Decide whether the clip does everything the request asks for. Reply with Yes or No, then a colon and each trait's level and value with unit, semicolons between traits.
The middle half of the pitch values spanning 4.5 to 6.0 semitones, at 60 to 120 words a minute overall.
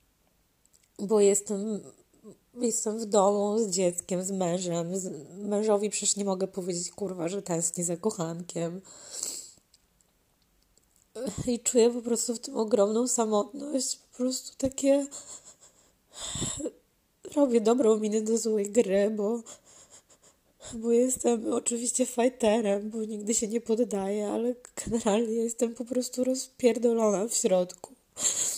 No: average, 3.6 semitones; average, 115 wpm